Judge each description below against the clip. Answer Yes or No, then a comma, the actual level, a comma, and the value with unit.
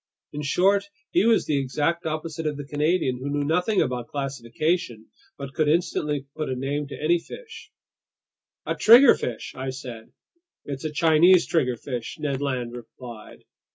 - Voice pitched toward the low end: No, medium, 145 Hz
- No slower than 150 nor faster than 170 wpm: Yes, average, 155 wpm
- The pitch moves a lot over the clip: No, average, 4.1 semitones